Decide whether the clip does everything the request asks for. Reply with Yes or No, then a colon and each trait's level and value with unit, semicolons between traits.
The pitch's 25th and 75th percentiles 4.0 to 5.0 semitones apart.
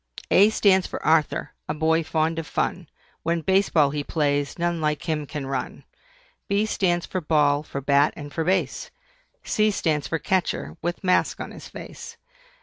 No: average, 3.5 semitones